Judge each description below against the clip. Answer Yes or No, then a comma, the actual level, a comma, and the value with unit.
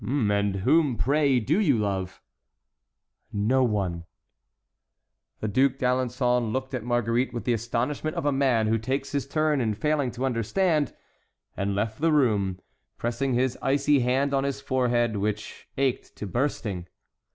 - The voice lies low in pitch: Yes, low, 125 Hz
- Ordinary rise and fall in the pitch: Yes, average, 4.1 semitones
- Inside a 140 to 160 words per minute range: Yes, average, 150 wpm